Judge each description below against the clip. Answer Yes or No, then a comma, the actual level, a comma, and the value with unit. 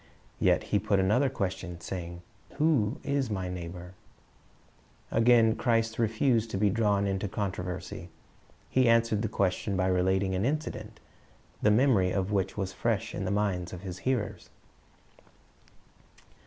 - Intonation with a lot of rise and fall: No, average, 3.5 semitones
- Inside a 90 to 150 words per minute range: Yes, average, 140 wpm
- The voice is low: Yes, low, 100 Hz